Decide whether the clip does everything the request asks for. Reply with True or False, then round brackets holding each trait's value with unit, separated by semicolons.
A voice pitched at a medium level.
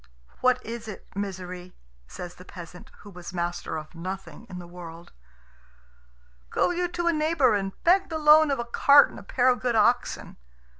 False (205 Hz)